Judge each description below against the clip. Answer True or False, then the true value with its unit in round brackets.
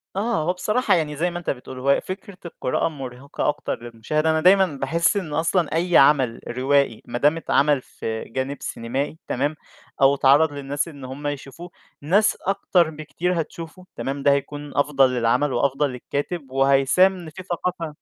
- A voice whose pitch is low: False (145 Hz)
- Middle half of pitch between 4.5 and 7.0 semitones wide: False (3.9 semitones)